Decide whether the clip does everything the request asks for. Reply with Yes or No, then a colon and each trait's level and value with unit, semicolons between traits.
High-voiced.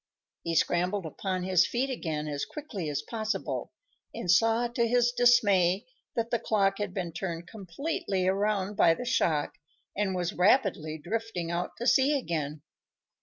Yes: high, 195 Hz